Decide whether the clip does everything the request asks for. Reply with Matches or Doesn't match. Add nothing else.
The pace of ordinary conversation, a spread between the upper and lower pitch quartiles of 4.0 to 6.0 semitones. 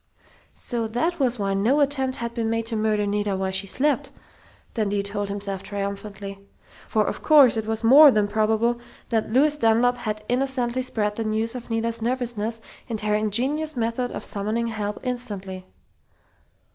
Doesn't match